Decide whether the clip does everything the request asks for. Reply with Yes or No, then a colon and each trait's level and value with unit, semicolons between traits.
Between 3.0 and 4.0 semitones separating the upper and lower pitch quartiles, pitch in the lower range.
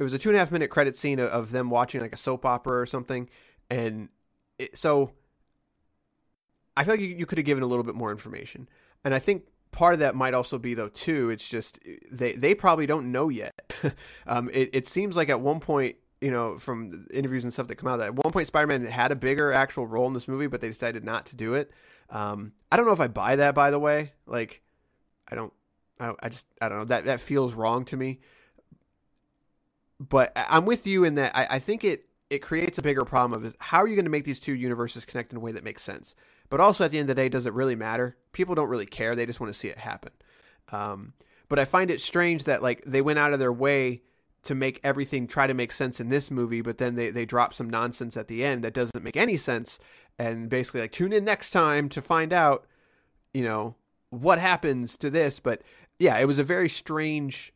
Yes: average, 3.4 semitones; low, 130 Hz